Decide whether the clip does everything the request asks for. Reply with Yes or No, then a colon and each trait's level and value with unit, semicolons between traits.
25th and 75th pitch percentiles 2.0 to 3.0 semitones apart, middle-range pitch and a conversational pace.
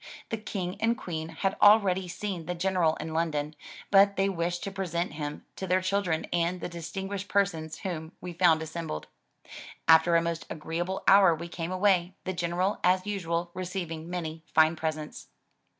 Yes: average, 2.7 semitones; medium, 175 Hz; average, 165 wpm